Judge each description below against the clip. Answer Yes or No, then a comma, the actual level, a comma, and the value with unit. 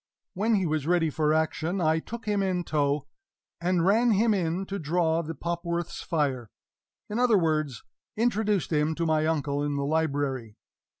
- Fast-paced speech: No, average, 170 wpm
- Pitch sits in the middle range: Yes, medium, 165 Hz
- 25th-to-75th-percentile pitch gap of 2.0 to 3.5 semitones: No, average, 4.1 semitones